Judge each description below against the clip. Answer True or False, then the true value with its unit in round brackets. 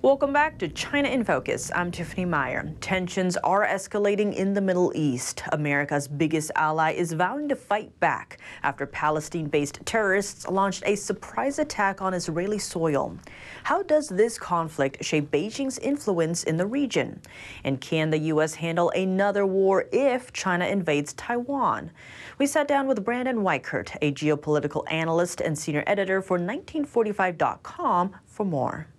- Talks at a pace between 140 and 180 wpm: True (145 wpm)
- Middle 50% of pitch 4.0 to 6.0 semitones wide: True (5.1 semitones)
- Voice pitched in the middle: True (180 Hz)